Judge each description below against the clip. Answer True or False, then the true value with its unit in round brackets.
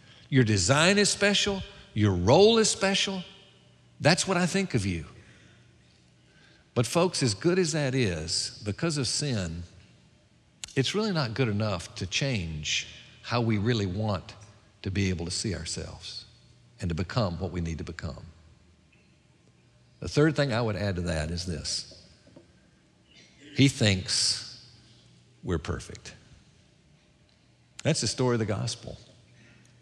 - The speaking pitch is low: True (110 Hz)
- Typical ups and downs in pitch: False (7.4 semitones)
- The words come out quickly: False (140 wpm)